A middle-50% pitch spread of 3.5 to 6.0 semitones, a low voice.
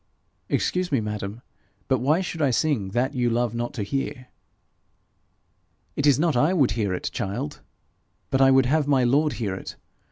Yes: average, 4.0 semitones; low, 130 Hz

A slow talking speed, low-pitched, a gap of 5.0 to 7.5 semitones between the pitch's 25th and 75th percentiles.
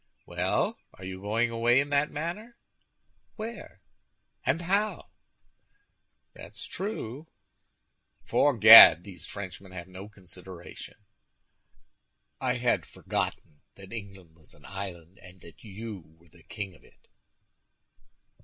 Yes: slow, 115 wpm; low, 100 Hz; wide, 5.6 semitones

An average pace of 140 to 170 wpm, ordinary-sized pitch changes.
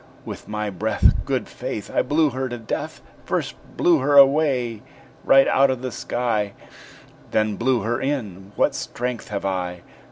Yes: average, 160 wpm; average, 4.3 semitones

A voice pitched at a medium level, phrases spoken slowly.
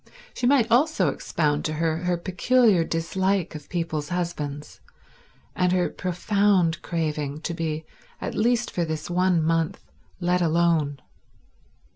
Yes: medium, 170 Hz; slow, 130 wpm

